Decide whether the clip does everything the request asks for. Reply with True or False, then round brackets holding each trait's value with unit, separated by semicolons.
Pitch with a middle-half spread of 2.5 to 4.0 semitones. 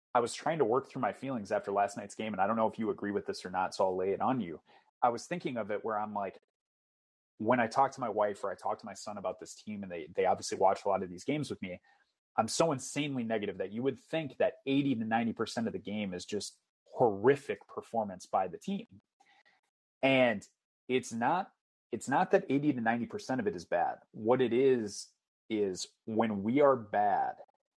False (4.5 semitones)